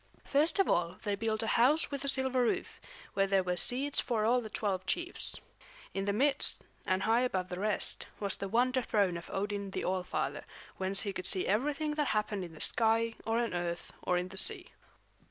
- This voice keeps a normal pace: No, fast, 215 wpm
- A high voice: Yes, high, 215 Hz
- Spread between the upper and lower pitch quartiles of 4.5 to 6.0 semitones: Yes, average, 4.8 semitones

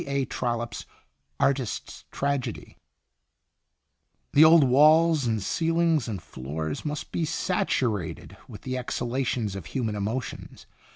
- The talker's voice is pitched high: No, low, 130 Hz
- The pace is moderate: No, slow, 120 wpm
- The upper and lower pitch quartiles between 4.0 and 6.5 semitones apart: Yes, average, 5.2 semitones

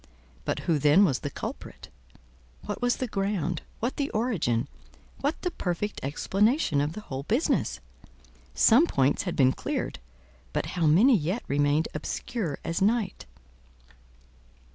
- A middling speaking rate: No, slow, 130 wpm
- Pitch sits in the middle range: Yes, medium, 180 Hz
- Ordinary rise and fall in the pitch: No, wide, 7.8 semitones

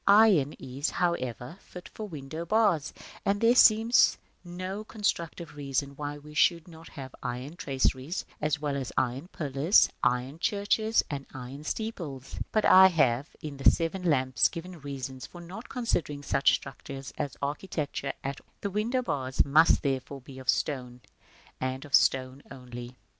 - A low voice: No, medium, 145 Hz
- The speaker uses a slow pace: No, average, 160 wpm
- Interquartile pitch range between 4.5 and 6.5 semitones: Yes, average, 5.2 semitones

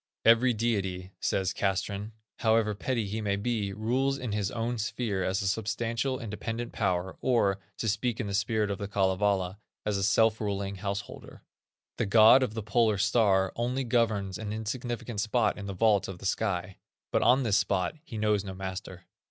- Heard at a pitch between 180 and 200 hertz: No, low, 105 Hz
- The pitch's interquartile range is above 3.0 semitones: No, average, 2.7 semitones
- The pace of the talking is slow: No, average, 180 wpm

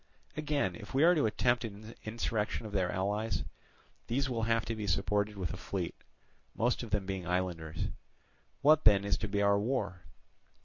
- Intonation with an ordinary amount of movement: Yes, average, 3.1 semitones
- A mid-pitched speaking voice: No, low, 105 Hz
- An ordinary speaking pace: Yes, average, 180 wpm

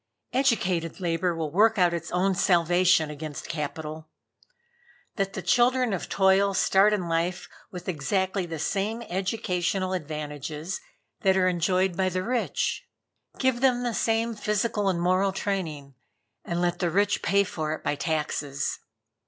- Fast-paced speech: No, average, 145 wpm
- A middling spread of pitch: Yes, average, 3.3 semitones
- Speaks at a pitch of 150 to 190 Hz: Yes, medium, 185 Hz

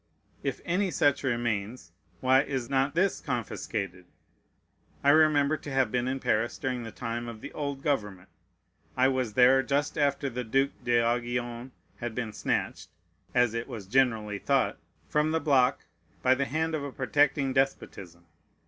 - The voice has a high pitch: No, low, 130 Hz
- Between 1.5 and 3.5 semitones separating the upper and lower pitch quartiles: Yes, average, 3.1 semitones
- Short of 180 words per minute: Yes, average, 155 wpm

